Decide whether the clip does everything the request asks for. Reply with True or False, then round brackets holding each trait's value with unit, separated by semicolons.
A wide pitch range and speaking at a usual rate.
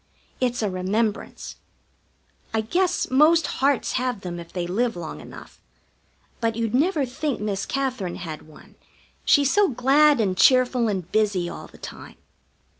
True (6.1 semitones; 150 wpm)